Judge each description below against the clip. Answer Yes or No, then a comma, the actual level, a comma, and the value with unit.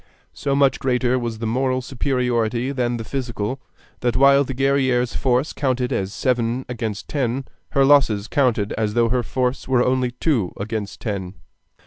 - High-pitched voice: No, low, 125 Hz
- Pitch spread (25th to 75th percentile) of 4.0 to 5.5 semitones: No, narrow, 2.5 semitones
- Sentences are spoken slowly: No, average, 160 wpm